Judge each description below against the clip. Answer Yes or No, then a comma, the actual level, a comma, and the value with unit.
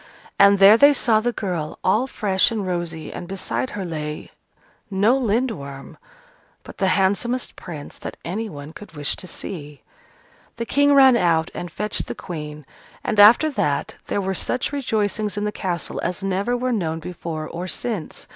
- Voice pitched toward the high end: Yes, high, 195 Hz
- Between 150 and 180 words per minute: Yes, average, 170 wpm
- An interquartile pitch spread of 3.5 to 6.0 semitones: Yes, average, 5.0 semitones